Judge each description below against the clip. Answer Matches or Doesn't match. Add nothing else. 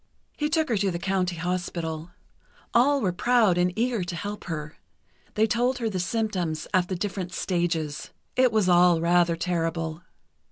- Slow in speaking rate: Doesn't match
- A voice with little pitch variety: Doesn't match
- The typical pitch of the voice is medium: Matches